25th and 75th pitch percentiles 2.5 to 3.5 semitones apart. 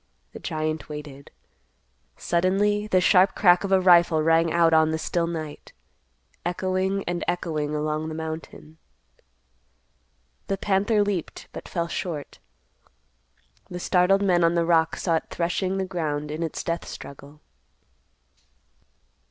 Yes: average, 2.9 semitones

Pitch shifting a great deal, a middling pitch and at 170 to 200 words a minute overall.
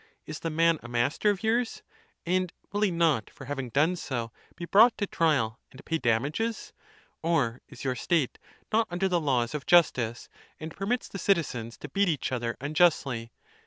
Yes: wide, 6.2 semitones; medium, 155 Hz; average, 180 wpm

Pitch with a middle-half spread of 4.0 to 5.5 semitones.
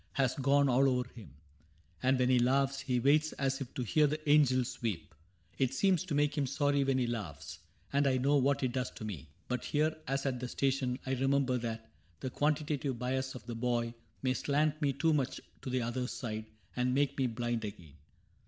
No: narrow, 2.5 semitones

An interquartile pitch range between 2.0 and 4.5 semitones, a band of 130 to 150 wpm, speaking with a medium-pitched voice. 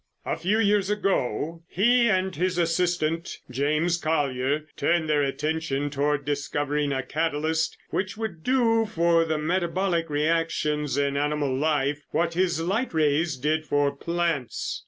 Yes: average, 3.1 semitones; slow, 135 wpm; medium, 160 Hz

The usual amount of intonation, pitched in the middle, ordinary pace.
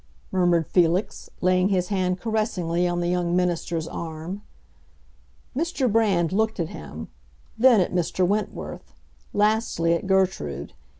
No: average, 3.3 semitones; medium, 180 Hz; slow, 125 wpm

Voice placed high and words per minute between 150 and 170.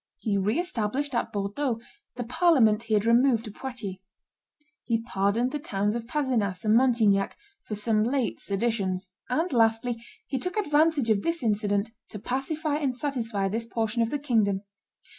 Yes: high, 230 Hz; average, 160 wpm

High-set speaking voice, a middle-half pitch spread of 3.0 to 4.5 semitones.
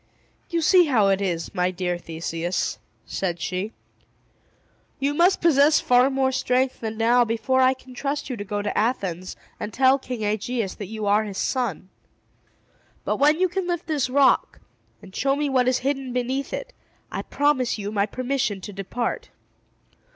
No: very high, 250 Hz; average, 5.3 semitones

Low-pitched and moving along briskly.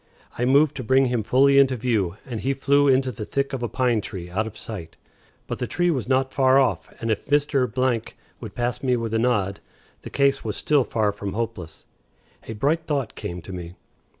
Yes: low, 125 Hz; fast, 210 wpm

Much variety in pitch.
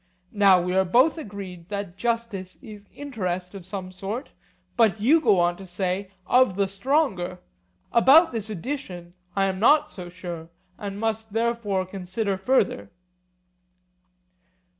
No: average, 4.0 semitones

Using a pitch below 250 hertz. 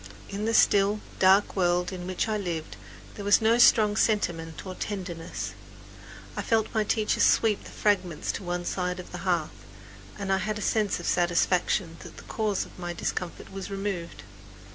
Yes: high, 190 Hz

